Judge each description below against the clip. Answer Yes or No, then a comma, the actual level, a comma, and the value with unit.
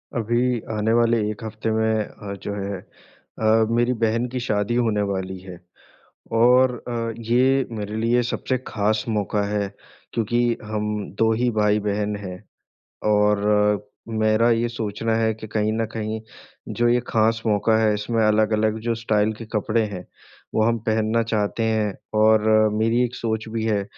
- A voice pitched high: No, low, 110 Hz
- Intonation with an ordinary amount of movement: No, narrow, 1.7 semitones